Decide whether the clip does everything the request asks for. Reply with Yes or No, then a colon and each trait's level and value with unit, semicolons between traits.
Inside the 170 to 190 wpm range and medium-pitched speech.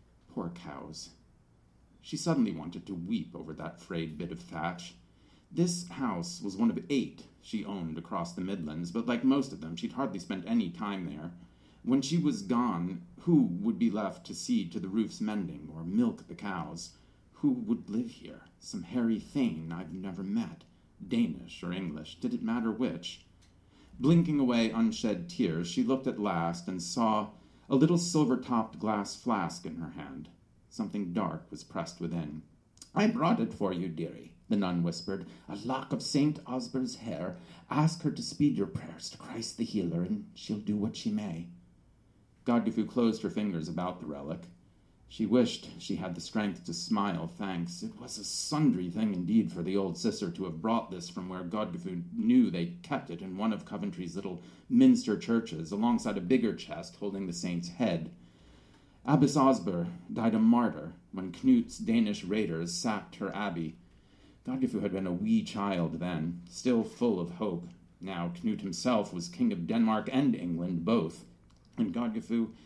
No: average, 175 wpm; low, 115 Hz